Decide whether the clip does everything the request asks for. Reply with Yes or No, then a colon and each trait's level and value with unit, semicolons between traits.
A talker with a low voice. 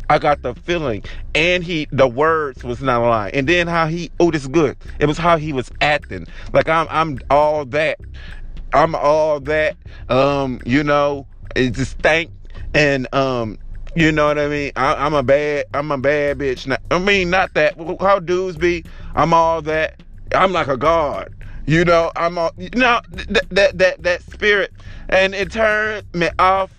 No: medium, 150 Hz